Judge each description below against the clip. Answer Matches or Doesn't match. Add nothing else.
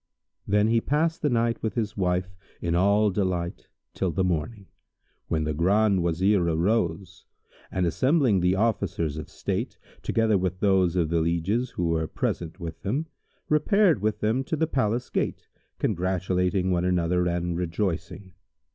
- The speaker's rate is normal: Matches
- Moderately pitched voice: Doesn't match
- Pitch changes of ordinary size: Matches